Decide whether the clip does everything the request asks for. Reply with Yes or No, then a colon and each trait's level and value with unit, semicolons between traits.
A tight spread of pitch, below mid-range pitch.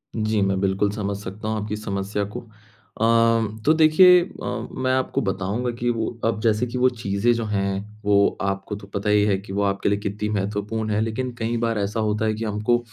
Yes: narrow, 2.2 semitones; low, 105 Hz